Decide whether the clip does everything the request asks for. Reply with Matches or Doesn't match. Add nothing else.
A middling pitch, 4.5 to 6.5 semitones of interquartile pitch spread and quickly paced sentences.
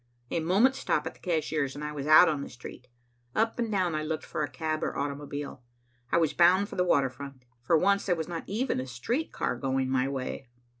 Matches